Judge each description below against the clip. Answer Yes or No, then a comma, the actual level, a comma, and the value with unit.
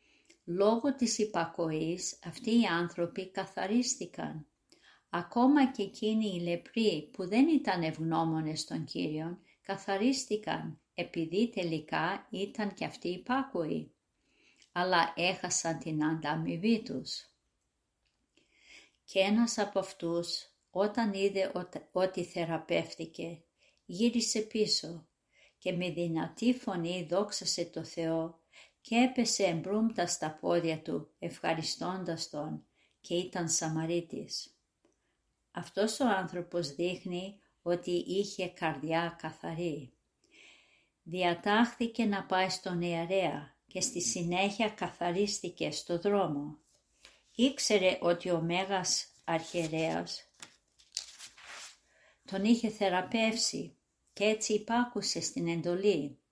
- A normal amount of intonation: Yes, average, 3.8 semitones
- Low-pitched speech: No, medium, 185 Hz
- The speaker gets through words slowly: Yes, slow, 95 wpm